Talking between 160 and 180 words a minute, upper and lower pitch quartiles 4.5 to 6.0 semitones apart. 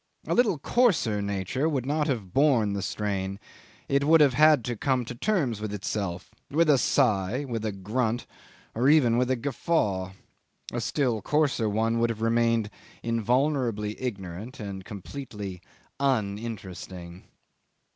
No: average, 145 wpm; average, 5.2 semitones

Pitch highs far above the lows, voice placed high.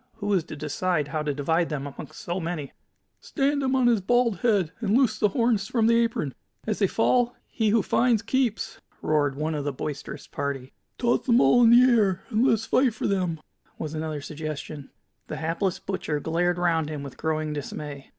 No: wide, 7.1 semitones; medium, 180 Hz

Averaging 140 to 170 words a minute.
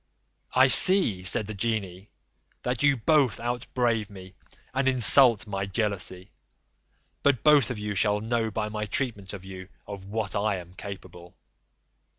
Yes: average, 155 wpm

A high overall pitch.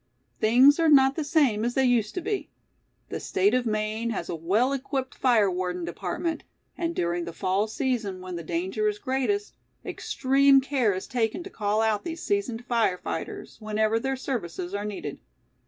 Yes: high, 225 Hz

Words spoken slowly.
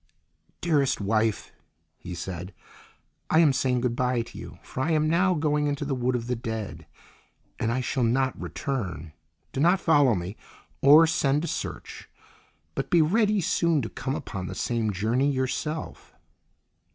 No: average, 165 wpm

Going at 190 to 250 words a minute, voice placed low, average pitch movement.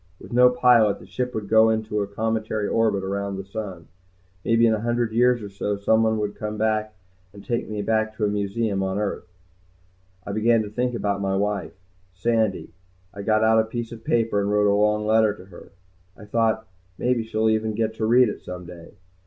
No: fast, 205 wpm; low, 110 Hz; narrow, 1.9 semitones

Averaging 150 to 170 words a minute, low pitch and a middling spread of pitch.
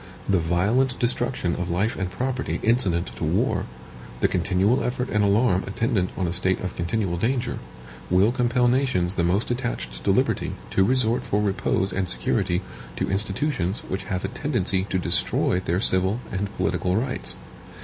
Yes: average, 165 wpm; low, 100 Hz; average, 4.8 semitones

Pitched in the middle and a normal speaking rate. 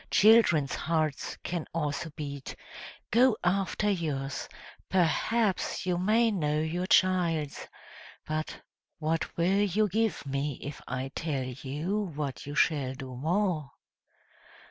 No: medium, 165 Hz; slow, 120 wpm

